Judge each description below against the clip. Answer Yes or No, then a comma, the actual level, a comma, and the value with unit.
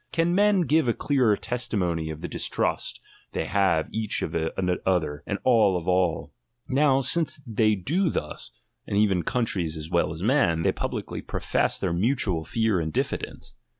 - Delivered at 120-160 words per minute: No, average, 170 wpm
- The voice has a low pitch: Yes, low, 100 Hz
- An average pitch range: No, wide, 7.1 semitones